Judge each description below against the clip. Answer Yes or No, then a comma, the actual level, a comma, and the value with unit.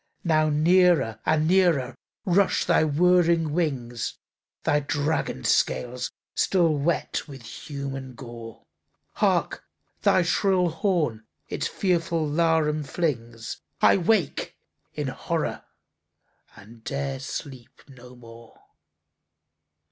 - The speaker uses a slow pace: Yes, slow, 100 wpm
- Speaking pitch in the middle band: Yes, medium, 150 Hz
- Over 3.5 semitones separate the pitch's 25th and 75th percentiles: Yes, wide, 5.4 semitones